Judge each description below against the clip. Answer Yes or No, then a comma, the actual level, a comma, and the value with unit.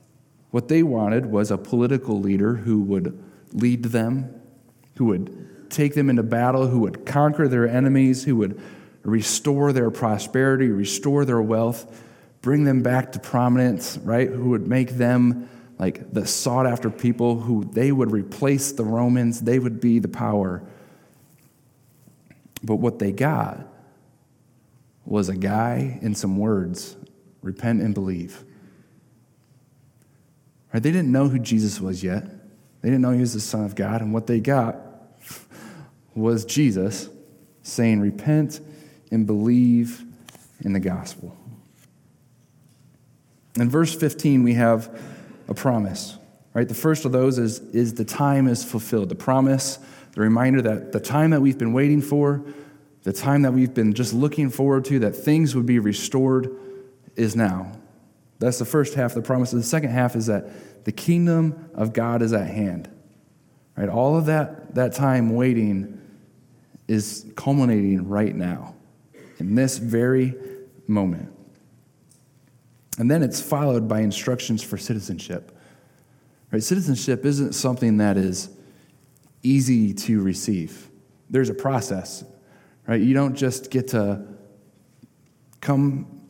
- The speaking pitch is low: Yes, low, 125 Hz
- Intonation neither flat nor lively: Yes, average, 3.5 semitones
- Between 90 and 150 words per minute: Yes, average, 140 wpm